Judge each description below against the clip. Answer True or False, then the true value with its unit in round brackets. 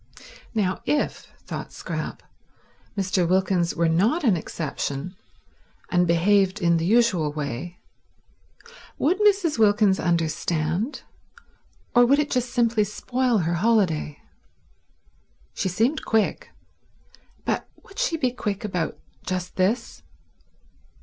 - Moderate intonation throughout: False (5.7 semitones)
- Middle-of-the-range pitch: False (195 Hz)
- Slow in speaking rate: True (110 wpm)